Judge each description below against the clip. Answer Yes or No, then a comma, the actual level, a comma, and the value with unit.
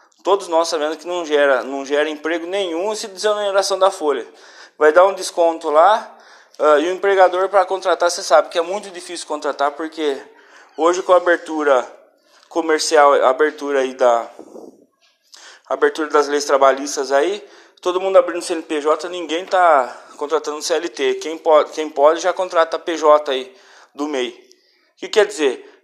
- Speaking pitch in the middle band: Yes, medium, 170 Hz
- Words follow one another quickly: No, average, 165 wpm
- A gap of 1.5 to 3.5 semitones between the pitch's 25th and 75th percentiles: No, average, 4.3 semitones